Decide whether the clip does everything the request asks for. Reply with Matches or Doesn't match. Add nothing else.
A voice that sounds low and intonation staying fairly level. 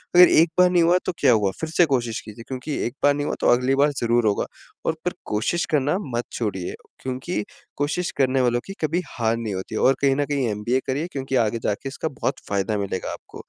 Doesn't match